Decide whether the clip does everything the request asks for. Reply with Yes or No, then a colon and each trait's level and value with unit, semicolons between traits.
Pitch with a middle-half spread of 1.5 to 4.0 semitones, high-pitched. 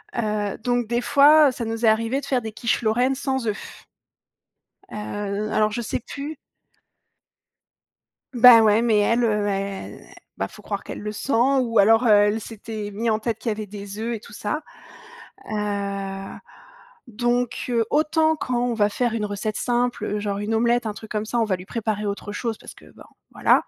Yes: average, 2.7 semitones; high, 225 Hz